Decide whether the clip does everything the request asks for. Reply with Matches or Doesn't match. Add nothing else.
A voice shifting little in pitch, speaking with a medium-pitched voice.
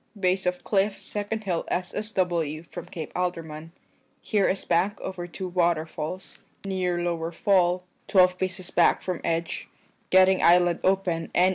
Matches